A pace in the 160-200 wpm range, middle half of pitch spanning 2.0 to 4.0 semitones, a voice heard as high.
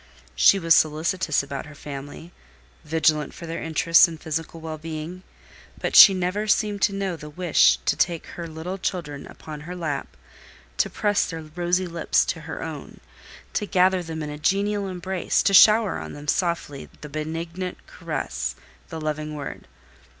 No: average, 165 wpm; average, 3.3 semitones; medium, 165 Hz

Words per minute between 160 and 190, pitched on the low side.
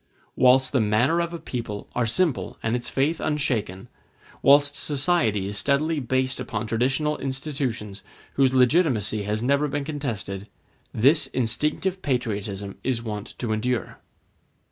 No: slow, 135 wpm; low, 130 Hz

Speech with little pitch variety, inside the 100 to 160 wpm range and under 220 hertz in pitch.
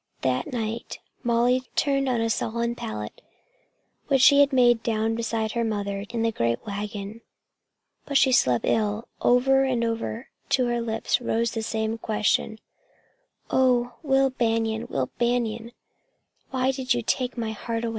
No: narrow, 2.2 semitones; average, 155 wpm; high, 230 Hz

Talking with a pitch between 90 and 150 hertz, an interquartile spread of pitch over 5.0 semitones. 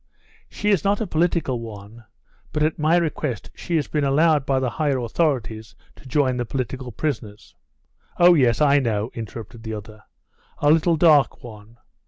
Yes: low, 135 Hz; wide, 5.4 semitones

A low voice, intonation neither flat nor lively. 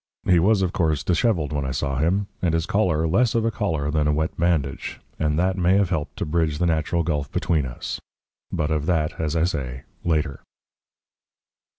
Yes: very low, 80 Hz; average, 3.1 semitones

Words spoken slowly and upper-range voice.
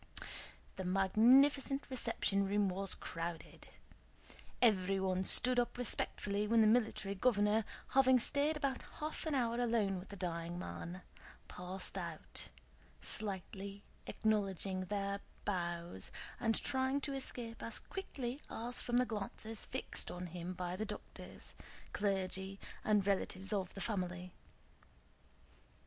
Yes: slow, 125 wpm; high, 200 Hz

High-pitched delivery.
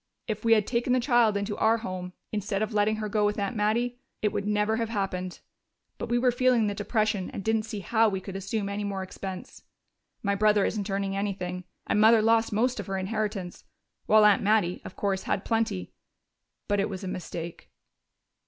Yes: high, 210 Hz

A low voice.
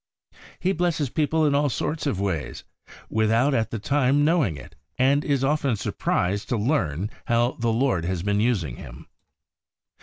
Yes: low, 120 Hz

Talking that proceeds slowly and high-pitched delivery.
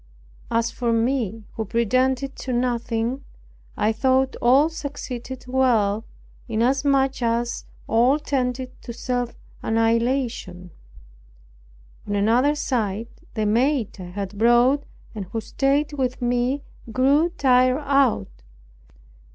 Yes: slow, 110 wpm; high, 245 Hz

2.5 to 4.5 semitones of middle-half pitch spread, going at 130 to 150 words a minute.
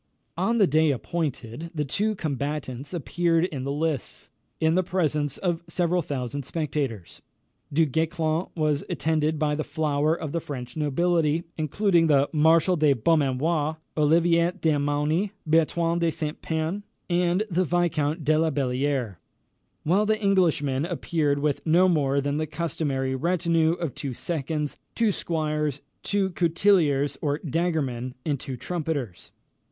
Yes: average, 2.9 semitones; average, 140 wpm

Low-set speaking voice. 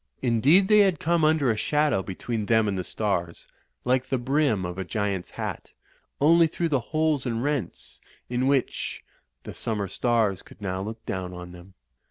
Yes: low, 115 Hz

